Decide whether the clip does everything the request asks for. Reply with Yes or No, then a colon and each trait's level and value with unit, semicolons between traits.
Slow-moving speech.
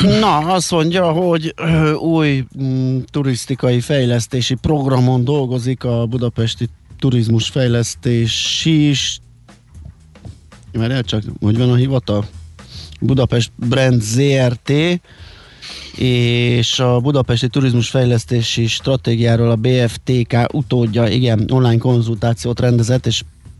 Yes: slow, 100 wpm